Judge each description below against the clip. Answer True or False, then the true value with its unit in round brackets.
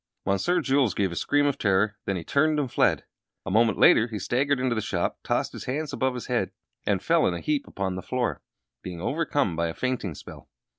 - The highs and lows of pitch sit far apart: True (6.5 semitones)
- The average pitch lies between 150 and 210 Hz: False (120 Hz)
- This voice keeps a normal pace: False (225 wpm)